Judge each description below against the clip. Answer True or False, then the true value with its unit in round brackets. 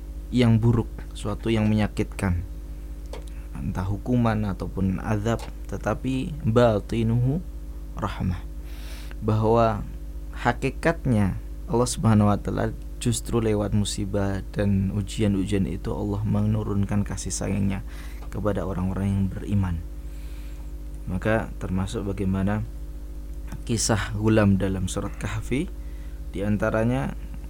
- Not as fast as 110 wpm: True (90 wpm)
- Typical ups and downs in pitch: False (6.2 semitones)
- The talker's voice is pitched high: False (100 Hz)